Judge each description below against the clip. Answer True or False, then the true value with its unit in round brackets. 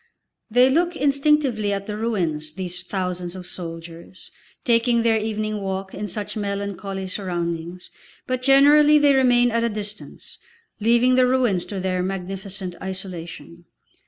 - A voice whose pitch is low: False (200 Hz)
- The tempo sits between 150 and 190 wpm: False (135 wpm)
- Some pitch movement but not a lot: True (4.8 semitones)